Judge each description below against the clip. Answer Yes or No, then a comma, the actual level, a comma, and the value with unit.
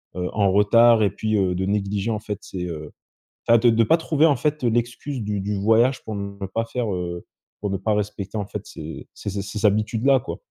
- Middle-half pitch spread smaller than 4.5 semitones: Yes, average, 2.9 semitones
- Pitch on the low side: Yes, low, 105 Hz